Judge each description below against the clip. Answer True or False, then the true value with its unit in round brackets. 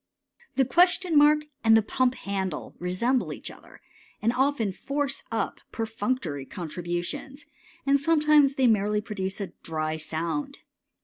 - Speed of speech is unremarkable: False (130 wpm)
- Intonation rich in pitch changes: True (7.1 semitones)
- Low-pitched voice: False (225 Hz)